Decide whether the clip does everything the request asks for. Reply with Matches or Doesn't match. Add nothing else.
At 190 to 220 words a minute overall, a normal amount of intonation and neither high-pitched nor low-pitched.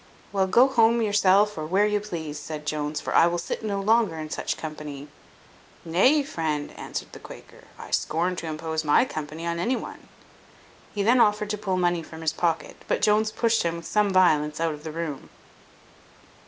Matches